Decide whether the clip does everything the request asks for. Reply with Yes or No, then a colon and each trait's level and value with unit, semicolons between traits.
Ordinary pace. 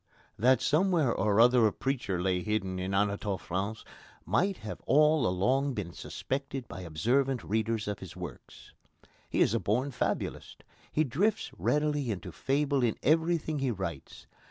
Yes: average, 155 wpm